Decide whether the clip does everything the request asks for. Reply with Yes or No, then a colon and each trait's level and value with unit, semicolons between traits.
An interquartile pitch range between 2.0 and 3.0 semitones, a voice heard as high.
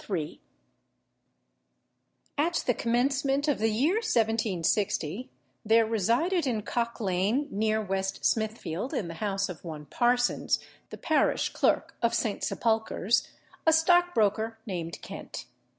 No: average, 4.6 semitones; high, 225 Hz